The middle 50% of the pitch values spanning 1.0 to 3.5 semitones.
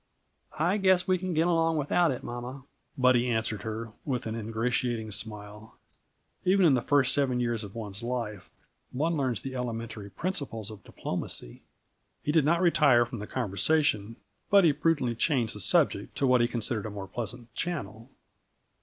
No: average, 5.2 semitones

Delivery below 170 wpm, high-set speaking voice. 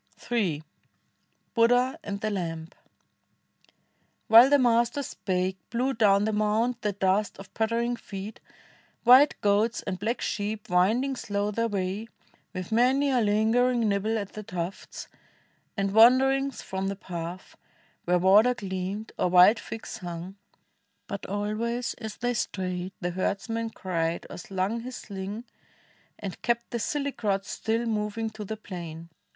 Yes: average, 140 wpm; high, 210 Hz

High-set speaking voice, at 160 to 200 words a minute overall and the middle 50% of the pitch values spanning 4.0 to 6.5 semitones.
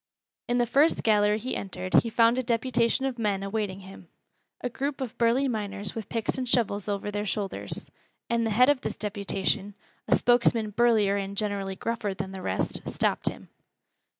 No: high, 215 Hz; average, 180 wpm; average, 3.1 semitones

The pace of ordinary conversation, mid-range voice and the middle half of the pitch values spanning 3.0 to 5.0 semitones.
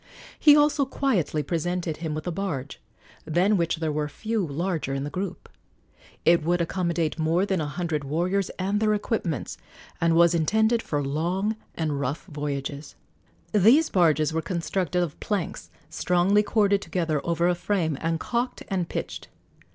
Yes: average, 160 wpm; medium, 170 Hz; average, 4.1 semitones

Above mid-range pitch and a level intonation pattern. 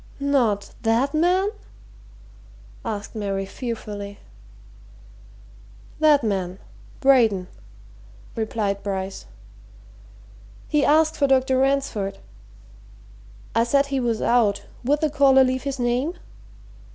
No: high, 245 Hz; average, 5.2 semitones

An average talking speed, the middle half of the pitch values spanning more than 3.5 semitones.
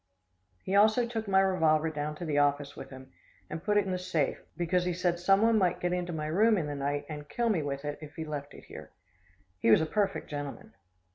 No: fast, 235 wpm; average, 4.6 semitones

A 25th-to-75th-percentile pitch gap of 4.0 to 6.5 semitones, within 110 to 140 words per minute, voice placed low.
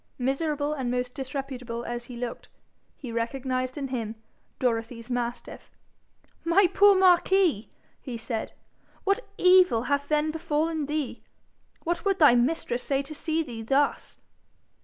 No: average, 4.7 semitones; slow, 135 wpm; very high, 270 Hz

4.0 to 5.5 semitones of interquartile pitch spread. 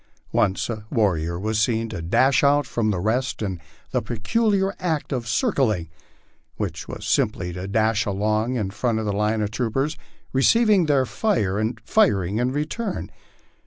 Yes: average, 5.0 semitones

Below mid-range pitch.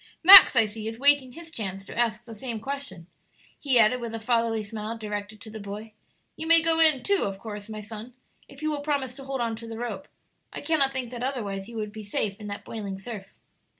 No: high, 230 Hz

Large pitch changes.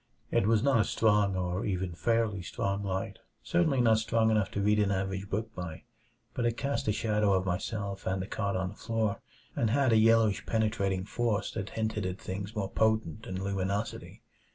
No: narrow, 2.5 semitones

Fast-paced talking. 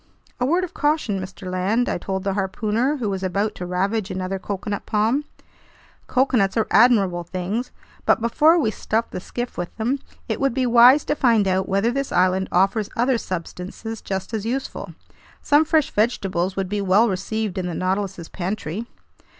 No: average, 175 wpm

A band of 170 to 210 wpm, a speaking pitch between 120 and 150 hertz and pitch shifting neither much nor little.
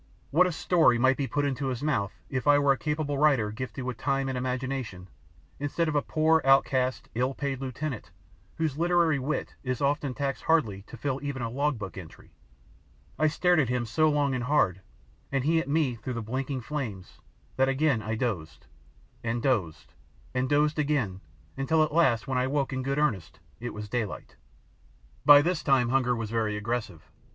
Yes: average, 190 wpm; low, 135 Hz; average, 3.7 semitones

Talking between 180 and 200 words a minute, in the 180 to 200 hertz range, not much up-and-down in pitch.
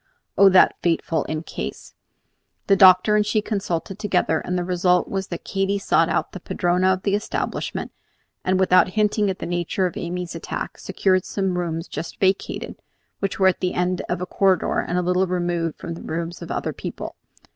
Yes: average, 190 wpm; medium, 185 Hz; narrow, 1.7 semitones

